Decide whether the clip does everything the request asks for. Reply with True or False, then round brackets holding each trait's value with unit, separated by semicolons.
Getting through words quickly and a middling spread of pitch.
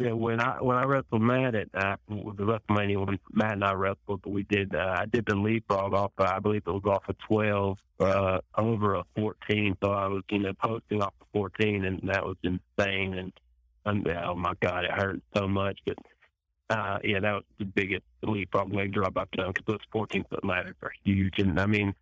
False (230 wpm; 1.7 semitones)